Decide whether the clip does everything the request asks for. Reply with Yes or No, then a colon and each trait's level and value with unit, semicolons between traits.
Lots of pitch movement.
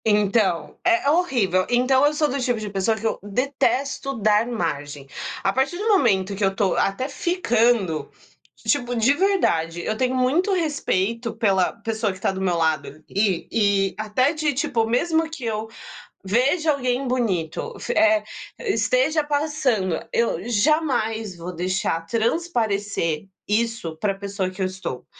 Yes: wide, 6.3 semitones